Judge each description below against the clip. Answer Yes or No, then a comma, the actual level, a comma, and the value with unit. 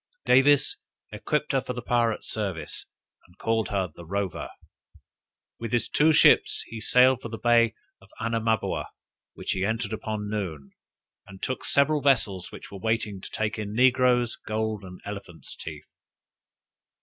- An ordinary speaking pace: Yes, average, 155 wpm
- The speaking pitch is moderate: No, low, 110 Hz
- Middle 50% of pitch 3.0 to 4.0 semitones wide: Yes, average, 3.7 semitones